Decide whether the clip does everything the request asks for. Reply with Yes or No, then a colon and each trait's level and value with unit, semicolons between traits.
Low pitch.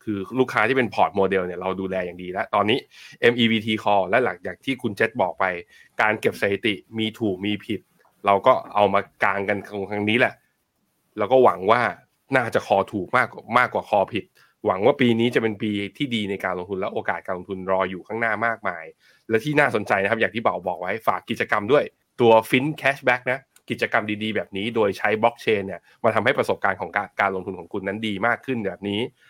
Yes: low, 105 Hz